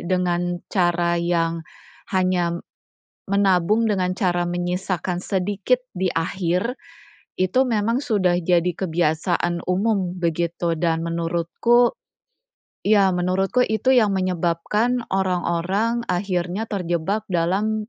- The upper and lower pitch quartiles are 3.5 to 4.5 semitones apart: No, average, 2.9 semitones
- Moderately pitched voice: Yes, medium, 180 Hz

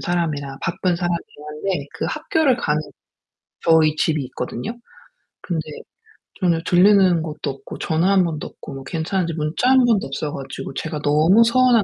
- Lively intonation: No, average, 4.4 semitones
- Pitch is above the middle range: No, medium, 170 Hz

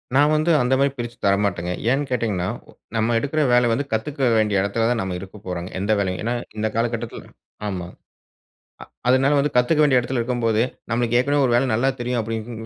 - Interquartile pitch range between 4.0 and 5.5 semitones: No, average, 3.5 semitones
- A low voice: Yes, low, 120 Hz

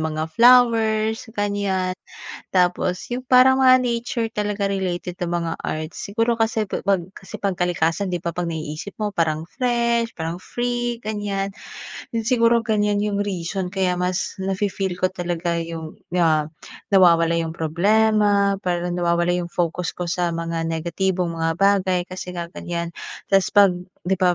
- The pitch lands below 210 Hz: Yes, medium, 185 Hz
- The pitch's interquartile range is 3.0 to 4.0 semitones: Yes, average, 3.6 semitones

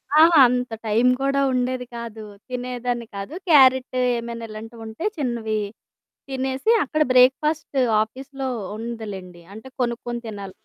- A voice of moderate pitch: No, high, 245 Hz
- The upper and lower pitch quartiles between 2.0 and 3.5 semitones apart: Yes, average, 2.8 semitones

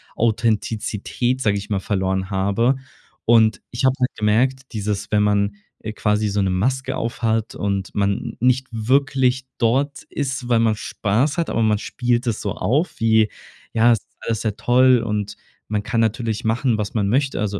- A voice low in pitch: Yes, low, 110 Hz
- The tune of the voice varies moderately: Yes, average, 3.3 semitones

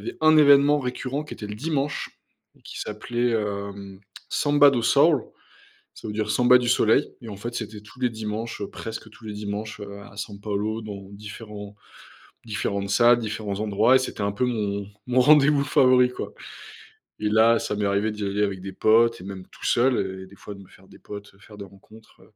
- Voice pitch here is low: Yes, low, 110 Hz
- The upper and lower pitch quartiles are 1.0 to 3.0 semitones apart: No, average, 3.4 semitones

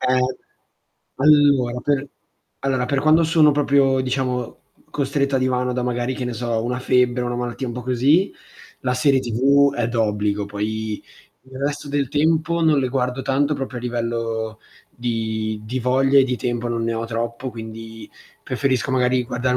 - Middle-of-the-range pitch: No, low, 125 Hz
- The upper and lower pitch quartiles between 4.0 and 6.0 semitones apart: No, average, 2.7 semitones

